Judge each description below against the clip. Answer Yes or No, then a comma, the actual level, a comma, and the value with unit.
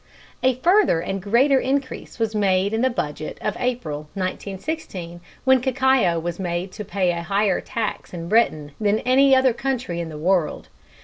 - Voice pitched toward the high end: Yes, high, 205 Hz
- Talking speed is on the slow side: No, average, 175 wpm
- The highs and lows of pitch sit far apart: Yes, wide, 6.8 semitones